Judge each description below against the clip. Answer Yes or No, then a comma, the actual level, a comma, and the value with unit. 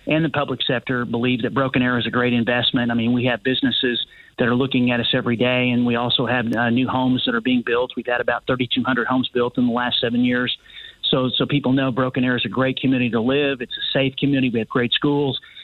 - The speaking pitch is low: Yes, low, 125 Hz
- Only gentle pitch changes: Yes, narrow, 1.3 semitones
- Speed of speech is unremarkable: No, fast, 260 wpm